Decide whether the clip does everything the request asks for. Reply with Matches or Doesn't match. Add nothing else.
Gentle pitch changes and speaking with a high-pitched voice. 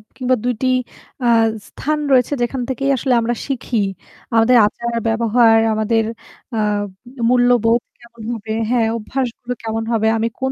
Matches